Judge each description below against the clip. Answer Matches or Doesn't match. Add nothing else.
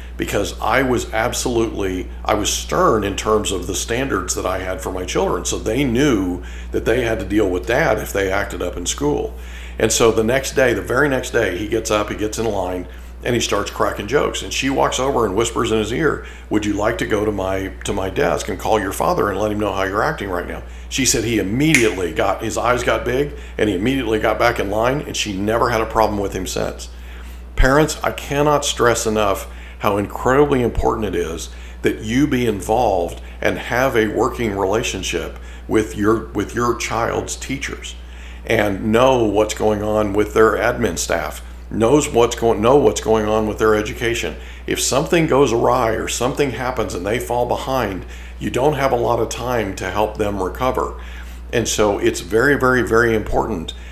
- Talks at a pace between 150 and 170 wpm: Doesn't match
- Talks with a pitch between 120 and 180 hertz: Doesn't match